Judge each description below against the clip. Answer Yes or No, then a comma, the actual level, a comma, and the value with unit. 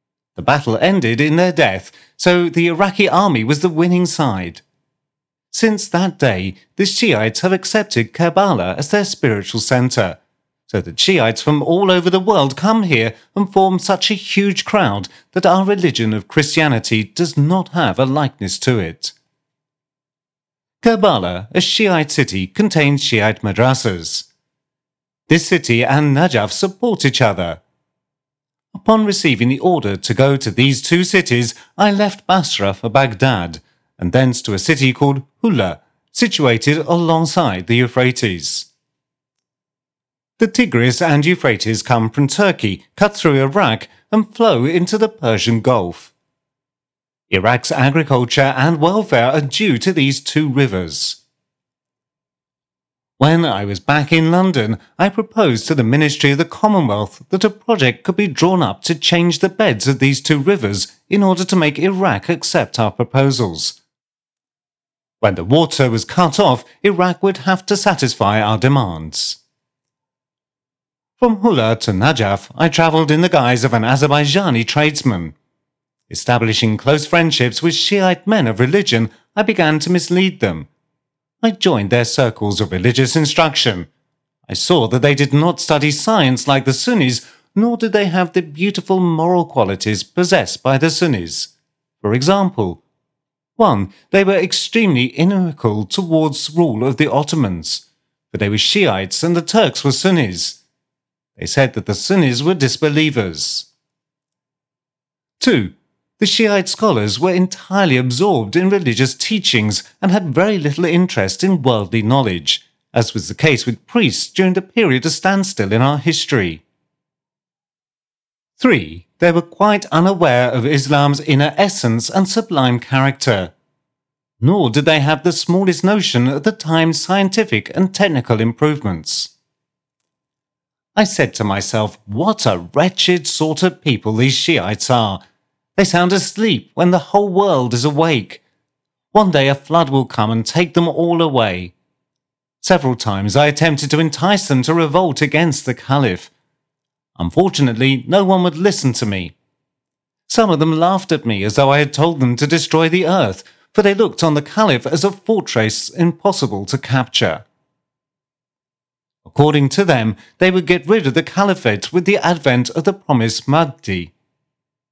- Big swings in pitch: Yes, wide, 6.9 semitones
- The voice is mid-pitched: Yes, medium, 150 Hz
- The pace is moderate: Yes, average, 150 wpm